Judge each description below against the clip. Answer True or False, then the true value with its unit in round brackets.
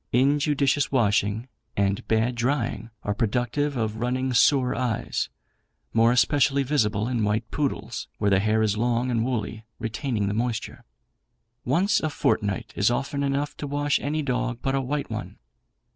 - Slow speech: False (155 wpm)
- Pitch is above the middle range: False (120 Hz)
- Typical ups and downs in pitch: True (3.9 semitones)